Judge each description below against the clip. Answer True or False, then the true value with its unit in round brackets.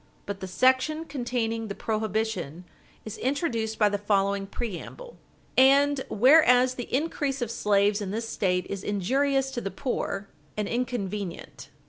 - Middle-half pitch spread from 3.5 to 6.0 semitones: True (4.6 semitones)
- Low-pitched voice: False (225 Hz)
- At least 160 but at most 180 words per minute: False (140 wpm)